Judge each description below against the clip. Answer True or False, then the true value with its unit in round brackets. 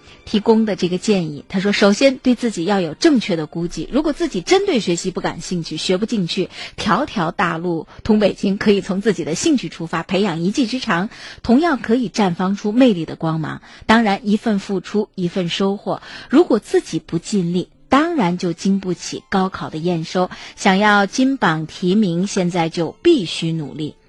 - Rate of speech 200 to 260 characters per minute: False (280 characters per minute)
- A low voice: False (195 Hz)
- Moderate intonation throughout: True (4.4 semitones)